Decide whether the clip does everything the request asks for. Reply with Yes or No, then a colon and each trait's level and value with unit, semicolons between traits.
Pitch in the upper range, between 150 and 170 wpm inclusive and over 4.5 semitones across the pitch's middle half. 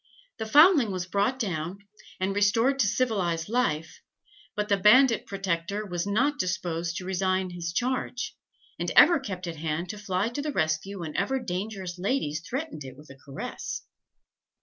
Yes: high, 195 Hz; average, 160 wpm; average, 5.3 semitones